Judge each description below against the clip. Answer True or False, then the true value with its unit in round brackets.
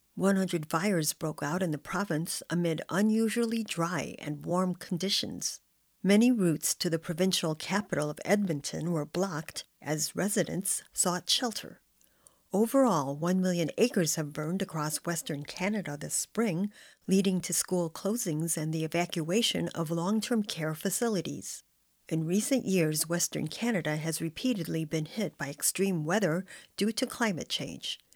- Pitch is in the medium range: True (180 Hz)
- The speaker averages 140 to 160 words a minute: True (145 wpm)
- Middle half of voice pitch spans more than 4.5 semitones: False (3.8 semitones)